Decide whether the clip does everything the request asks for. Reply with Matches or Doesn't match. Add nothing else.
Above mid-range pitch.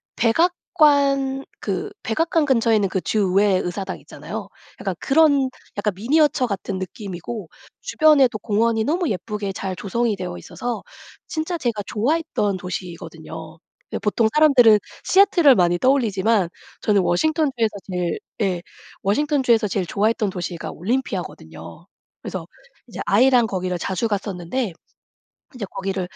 Matches